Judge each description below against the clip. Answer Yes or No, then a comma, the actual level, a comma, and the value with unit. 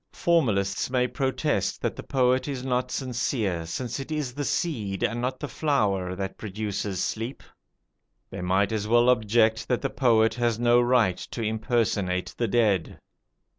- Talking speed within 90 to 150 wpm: No, average, 160 wpm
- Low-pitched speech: Yes, low, 115 Hz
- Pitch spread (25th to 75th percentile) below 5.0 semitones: Yes, average, 4.0 semitones